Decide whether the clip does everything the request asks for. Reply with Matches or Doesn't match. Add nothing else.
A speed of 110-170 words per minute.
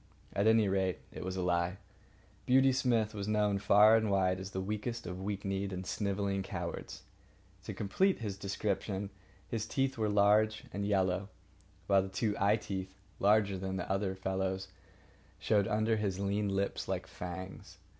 Matches